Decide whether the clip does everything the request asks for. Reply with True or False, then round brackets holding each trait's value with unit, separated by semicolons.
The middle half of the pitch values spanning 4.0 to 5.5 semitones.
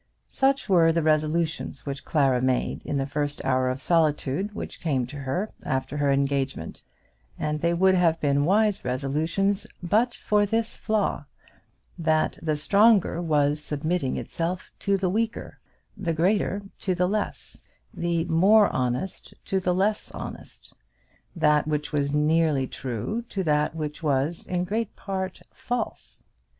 True (4.9 semitones)